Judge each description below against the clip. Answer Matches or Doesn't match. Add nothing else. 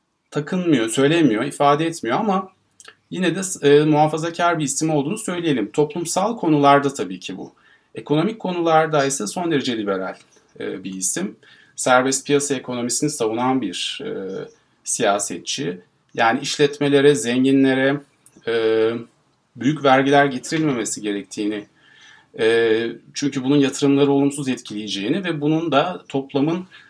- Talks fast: Doesn't match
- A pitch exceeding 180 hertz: Doesn't match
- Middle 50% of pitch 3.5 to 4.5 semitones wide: Matches